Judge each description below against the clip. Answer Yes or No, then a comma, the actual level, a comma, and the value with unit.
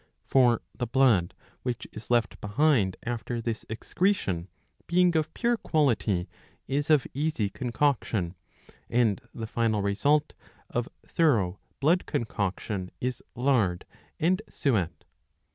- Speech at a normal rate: No, slow, 115 wpm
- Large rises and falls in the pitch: Yes, wide, 6.0 semitones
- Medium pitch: No, low, 120 Hz